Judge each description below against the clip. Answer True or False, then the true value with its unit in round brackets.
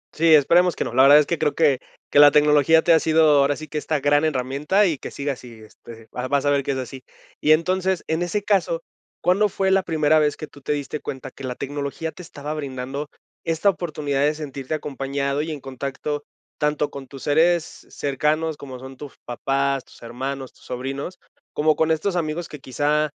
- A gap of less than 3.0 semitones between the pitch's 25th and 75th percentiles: True (2.6 semitones)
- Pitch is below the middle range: False (145 Hz)